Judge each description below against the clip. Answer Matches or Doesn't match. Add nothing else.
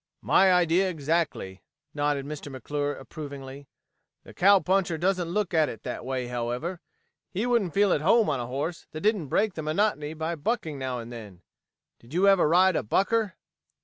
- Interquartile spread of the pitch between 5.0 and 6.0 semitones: Matches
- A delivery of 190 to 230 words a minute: Doesn't match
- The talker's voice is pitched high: Doesn't match